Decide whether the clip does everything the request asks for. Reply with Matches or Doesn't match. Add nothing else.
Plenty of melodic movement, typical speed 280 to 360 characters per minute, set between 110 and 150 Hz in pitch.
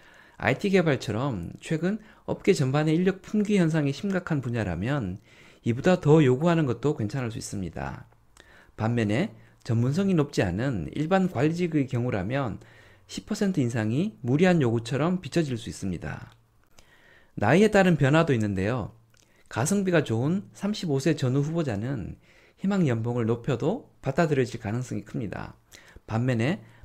Matches